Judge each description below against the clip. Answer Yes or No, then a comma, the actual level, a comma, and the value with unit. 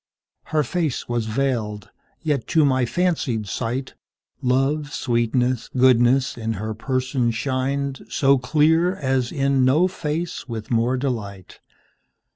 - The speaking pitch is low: Yes, low, 130 Hz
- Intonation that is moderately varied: Yes, average, 3.2 semitones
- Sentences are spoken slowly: Yes, slow, 110 wpm